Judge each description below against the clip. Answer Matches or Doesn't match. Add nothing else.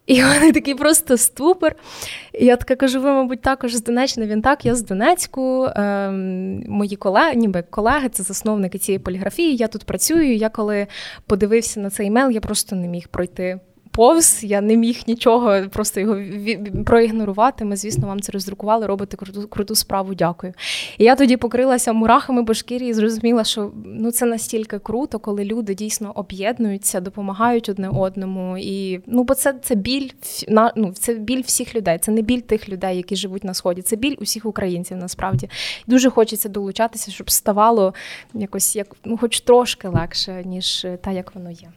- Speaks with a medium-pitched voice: Doesn't match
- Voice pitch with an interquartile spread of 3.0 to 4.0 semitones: Matches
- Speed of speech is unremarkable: Doesn't match